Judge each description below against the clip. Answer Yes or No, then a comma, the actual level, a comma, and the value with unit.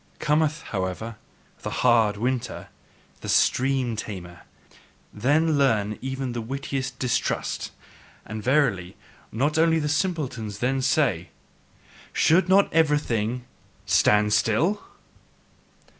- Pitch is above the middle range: No, low, 130 Hz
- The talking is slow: Yes, slow, 100 wpm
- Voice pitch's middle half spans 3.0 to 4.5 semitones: No, wide, 5.4 semitones